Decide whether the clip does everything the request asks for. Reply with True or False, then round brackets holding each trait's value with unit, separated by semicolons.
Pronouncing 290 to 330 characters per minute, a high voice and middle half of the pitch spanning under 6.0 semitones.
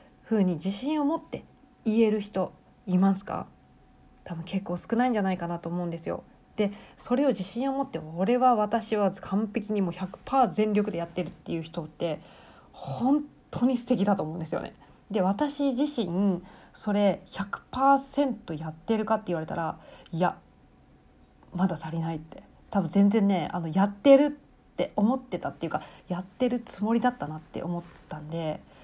True (320 characters per minute; 200 Hz; 5.5 semitones)